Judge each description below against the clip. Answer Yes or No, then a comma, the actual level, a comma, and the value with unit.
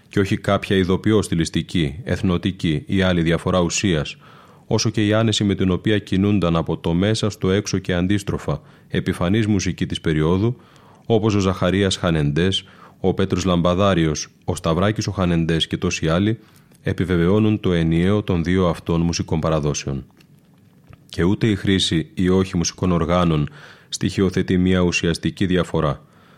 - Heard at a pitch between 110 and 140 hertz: No, very low, 95 Hz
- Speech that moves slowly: No, average, 145 wpm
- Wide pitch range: No, average, 3.0 semitones